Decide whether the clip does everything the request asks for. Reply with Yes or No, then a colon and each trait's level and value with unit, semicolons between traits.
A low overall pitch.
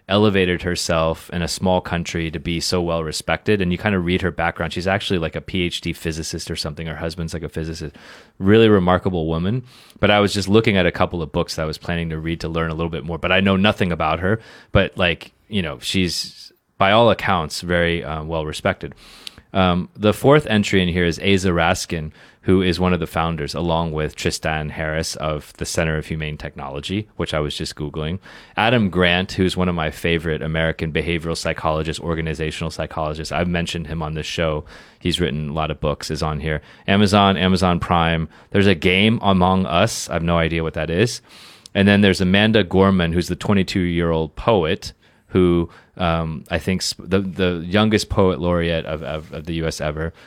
Yes: very low, 85 Hz